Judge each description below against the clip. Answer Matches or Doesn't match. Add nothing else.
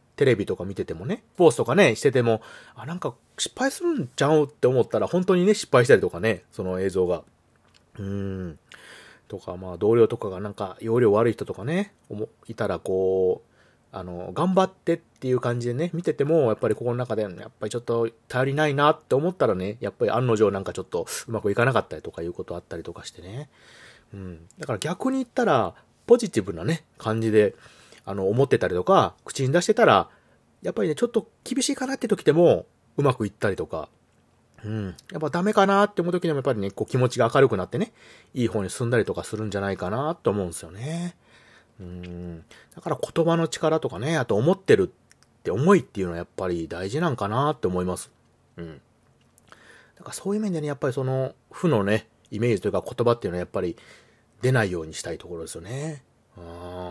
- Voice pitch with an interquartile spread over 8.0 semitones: Matches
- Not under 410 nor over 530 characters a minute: Matches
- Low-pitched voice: Matches